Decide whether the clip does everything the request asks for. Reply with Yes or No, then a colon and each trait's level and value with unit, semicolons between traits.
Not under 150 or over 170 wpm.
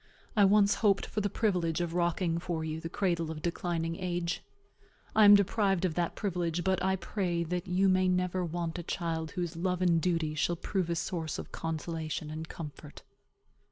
No: average, 190 wpm